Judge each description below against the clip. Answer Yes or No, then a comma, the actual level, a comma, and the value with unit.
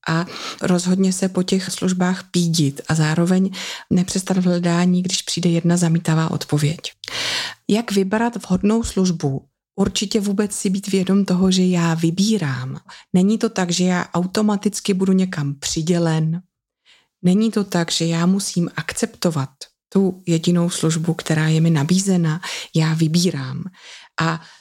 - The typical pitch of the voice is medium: Yes, medium, 180 Hz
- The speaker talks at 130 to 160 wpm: Yes, average, 135 wpm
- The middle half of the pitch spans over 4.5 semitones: No, average, 2.8 semitones